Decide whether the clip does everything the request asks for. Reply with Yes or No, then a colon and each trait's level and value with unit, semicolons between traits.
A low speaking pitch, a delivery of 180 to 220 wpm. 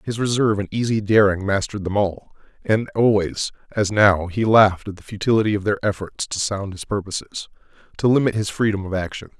Yes: low, 105 Hz; average, 190 wpm